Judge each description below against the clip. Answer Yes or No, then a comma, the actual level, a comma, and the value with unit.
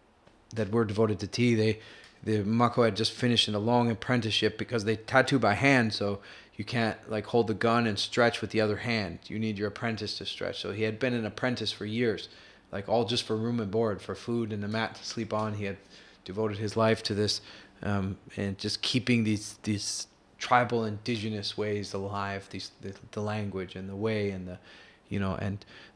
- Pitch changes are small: Yes, narrow, 2.1 semitones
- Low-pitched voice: Yes, low, 110 Hz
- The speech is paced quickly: Yes, fast, 210 wpm